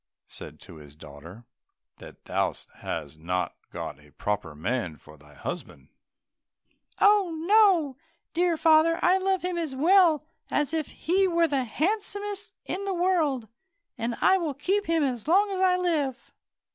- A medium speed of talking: Yes, average, 160 wpm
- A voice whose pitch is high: Yes, very high, 320 Hz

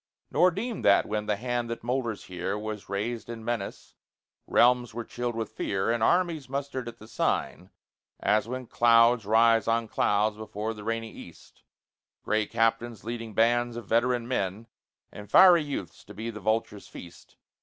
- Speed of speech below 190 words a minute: Yes, average, 165 wpm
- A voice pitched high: No, low, 115 Hz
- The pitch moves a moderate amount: No, narrow, 2.1 semitones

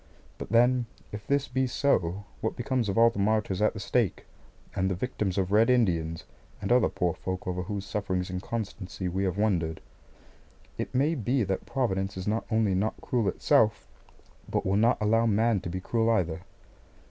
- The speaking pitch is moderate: No, low, 105 Hz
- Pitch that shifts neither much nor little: Yes, average, 3.7 semitones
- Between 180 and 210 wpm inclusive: Yes, average, 185 wpm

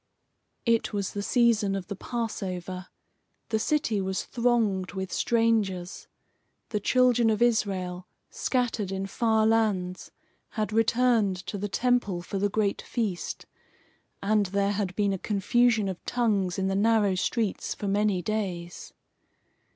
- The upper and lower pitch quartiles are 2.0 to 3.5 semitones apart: Yes, average, 3.1 semitones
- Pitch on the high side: Yes, high, 205 Hz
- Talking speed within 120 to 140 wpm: Yes, slow, 135 wpm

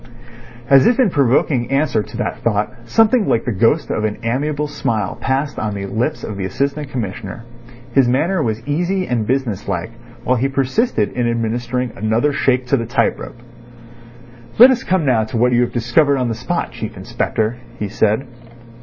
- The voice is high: No, low, 125 Hz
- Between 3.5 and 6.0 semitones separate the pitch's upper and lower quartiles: Yes, average, 4.2 semitones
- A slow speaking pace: No, average, 185 wpm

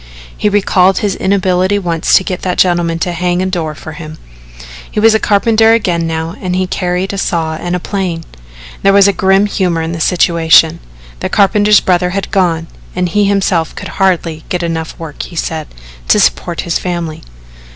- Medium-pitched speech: Yes, medium, 180 Hz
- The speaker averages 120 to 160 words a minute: No, average, 185 wpm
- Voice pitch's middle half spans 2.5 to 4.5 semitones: Yes, average, 2.9 semitones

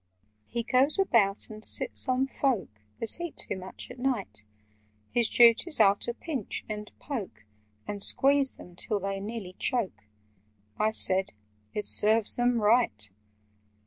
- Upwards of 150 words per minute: No, average, 145 wpm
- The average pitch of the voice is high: Yes, high, 225 Hz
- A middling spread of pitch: Yes, average, 4.3 semitones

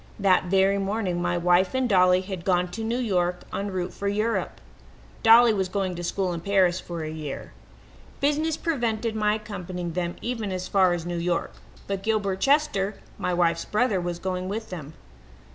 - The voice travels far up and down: No, average, 3.4 semitones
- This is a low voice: No, high, 190 Hz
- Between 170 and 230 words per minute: Yes, average, 180 wpm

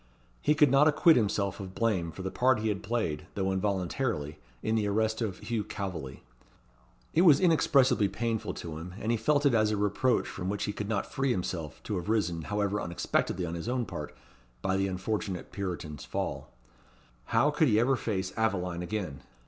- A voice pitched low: Yes, low, 105 Hz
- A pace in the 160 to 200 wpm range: Yes, average, 190 wpm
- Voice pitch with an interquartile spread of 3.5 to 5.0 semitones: Yes, average, 4.2 semitones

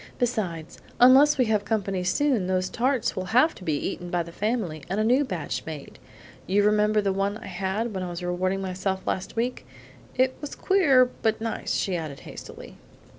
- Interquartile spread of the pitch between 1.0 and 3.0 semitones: No, average, 4.8 semitones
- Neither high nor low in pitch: No, high, 200 Hz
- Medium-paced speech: Yes, average, 190 wpm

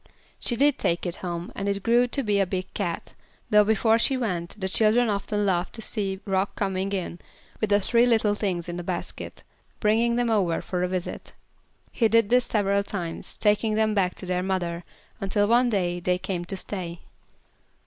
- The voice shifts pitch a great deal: No, average, 3.3 semitones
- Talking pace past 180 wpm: Yes, average, 195 wpm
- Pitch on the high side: Yes, high, 200 Hz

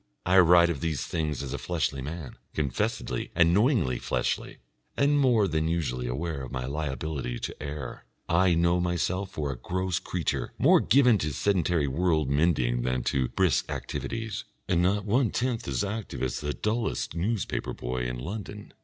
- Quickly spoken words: No, average, 170 wpm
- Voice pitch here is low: Yes, very low, 85 Hz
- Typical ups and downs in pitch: No, wide, 5.9 semitones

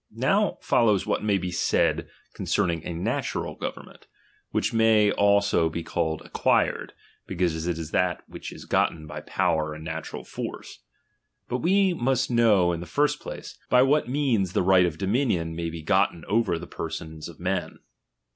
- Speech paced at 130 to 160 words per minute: No, average, 170 wpm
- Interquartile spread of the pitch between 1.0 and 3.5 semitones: No, wide, 5.4 semitones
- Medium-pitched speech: No, very low, 90 Hz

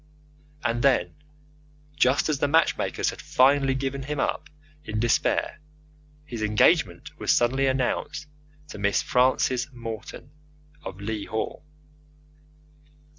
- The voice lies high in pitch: No, low, 130 Hz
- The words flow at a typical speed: No, slow, 115 wpm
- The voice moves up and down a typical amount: Yes, average, 3.9 semitones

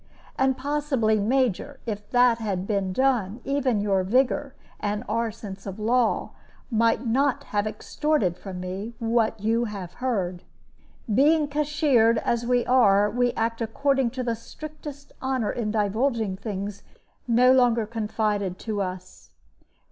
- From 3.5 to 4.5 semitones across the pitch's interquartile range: Yes, average, 4.0 semitones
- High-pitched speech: Yes, high, 230 Hz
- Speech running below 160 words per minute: Yes, average, 140 wpm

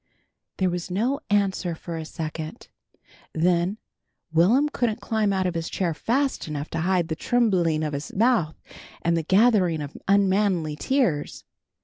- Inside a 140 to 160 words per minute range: Yes, average, 150 wpm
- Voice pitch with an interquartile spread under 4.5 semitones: No, average, 4.8 semitones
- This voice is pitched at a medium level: Yes, medium, 180 Hz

